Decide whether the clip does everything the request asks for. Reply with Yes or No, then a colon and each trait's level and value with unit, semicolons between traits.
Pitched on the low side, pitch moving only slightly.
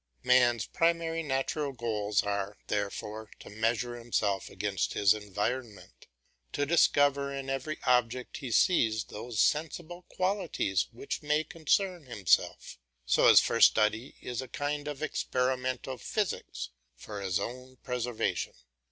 No: low, 125 Hz; average, 5.2 semitones